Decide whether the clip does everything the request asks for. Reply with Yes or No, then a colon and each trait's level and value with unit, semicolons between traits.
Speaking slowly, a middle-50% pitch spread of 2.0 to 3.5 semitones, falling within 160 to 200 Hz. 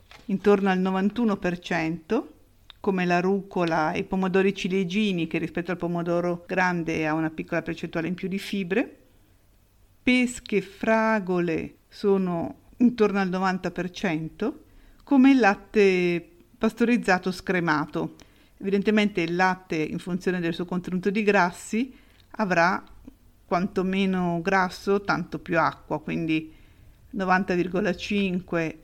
Yes: slow, 110 wpm; average, 3.0 semitones; medium, 185 Hz